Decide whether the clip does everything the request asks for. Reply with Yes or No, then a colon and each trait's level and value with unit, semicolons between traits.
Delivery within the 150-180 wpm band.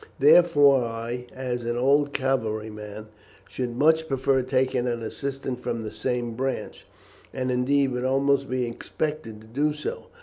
Yes: average, 155 wpm